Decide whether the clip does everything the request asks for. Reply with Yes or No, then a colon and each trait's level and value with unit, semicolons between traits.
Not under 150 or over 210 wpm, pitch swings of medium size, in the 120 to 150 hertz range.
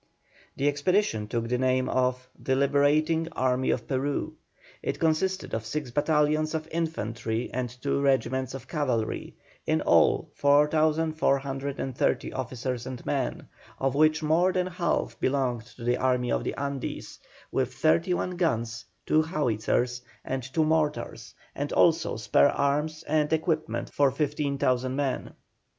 No: slow, 135 wpm; average, 3.5 semitones; medium, 140 Hz